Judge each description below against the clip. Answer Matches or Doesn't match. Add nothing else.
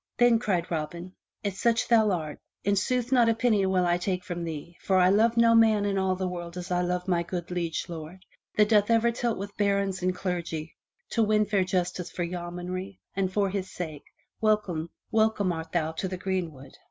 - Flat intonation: Doesn't match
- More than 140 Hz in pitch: Matches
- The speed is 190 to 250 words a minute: Matches